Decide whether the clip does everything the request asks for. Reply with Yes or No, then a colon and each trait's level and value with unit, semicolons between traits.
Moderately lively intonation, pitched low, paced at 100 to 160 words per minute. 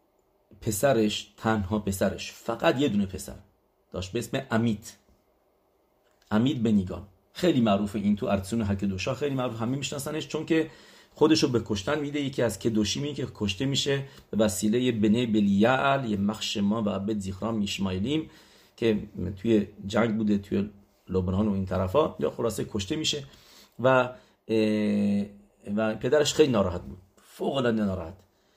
Yes: average, 3.9 semitones; low, 110 Hz; average, 145 wpm